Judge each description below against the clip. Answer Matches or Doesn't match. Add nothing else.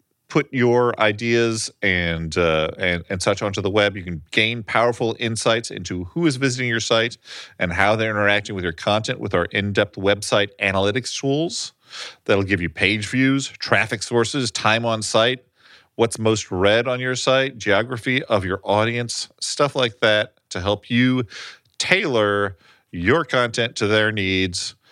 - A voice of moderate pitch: Doesn't match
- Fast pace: Doesn't match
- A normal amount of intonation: Matches